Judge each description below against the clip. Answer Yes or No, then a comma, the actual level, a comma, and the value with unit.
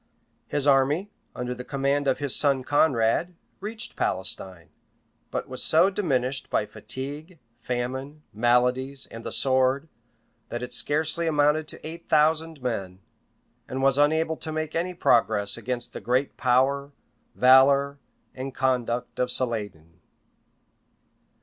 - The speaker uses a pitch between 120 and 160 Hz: Yes, low, 135 Hz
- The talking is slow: Yes, slow, 130 wpm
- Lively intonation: No, average, 3.5 semitones